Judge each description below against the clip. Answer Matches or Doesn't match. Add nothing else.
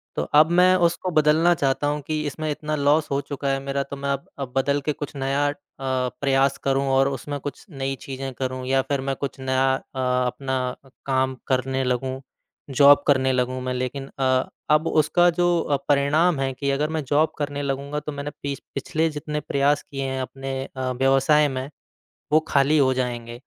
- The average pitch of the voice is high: Doesn't match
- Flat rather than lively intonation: Matches